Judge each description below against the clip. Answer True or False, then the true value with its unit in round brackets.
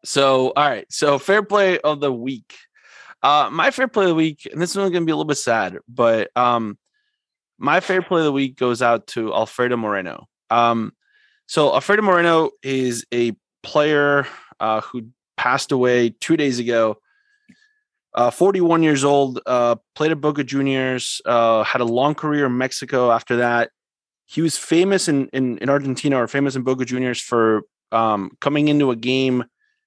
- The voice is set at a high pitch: False (140 Hz)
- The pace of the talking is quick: False (175 wpm)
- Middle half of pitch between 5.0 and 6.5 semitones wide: True (5.5 semitones)